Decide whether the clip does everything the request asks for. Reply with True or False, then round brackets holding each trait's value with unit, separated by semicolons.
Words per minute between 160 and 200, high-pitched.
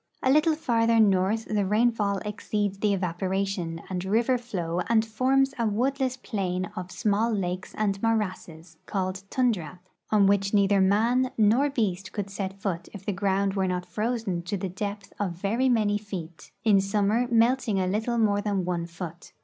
True (170 wpm; 200 Hz)